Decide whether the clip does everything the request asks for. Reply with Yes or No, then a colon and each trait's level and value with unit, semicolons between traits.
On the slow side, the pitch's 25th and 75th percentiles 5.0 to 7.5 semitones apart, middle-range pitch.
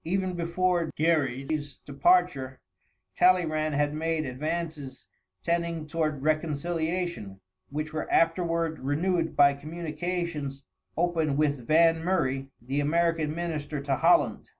No: slow, 105 wpm; average, 2.8 semitones; medium, 155 Hz